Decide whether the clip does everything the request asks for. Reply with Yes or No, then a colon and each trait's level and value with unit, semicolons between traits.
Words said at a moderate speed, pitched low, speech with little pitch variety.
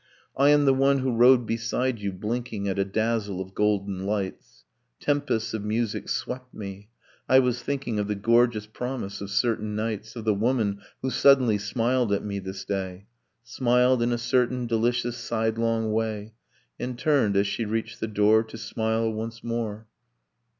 No: average, 170 wpm; low, 115 Hz; average, 3.0 semitones